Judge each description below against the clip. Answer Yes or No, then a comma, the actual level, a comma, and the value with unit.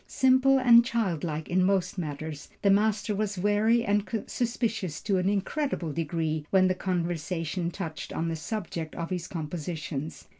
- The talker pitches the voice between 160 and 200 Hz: Yes, medium, 185 Hz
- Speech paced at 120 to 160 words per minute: Yes, average, 150 wpm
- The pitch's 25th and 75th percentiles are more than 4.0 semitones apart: Yes, average, 4.4 semitones